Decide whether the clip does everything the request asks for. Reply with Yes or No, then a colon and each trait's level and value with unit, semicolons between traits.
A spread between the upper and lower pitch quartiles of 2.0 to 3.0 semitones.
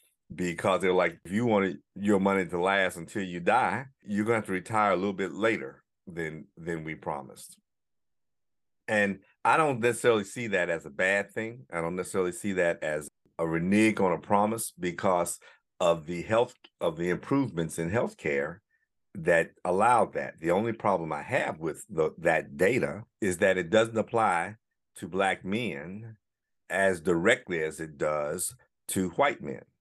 No: average, 3.9 semitones